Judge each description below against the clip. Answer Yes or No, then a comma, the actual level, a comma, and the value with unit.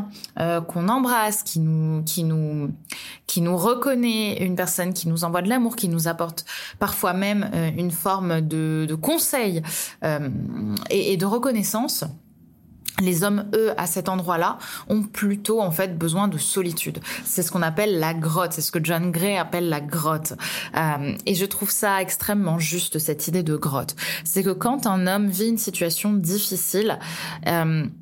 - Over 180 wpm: No, average, 175 wpm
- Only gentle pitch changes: No, average, 3.9 semitones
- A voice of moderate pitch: Yes, medium, 180 Hz